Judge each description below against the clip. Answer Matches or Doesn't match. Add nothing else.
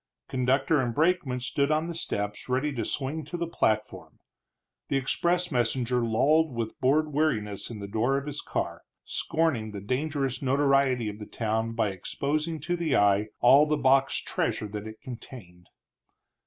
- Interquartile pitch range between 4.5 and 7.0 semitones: Matches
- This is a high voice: Doesn't match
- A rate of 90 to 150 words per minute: Doesn't match